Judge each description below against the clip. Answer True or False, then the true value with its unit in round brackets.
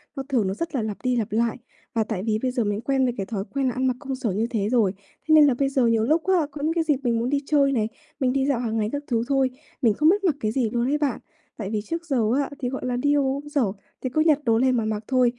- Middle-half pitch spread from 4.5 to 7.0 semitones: False (4.0 semitones)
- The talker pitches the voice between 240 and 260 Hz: True (255 Hz)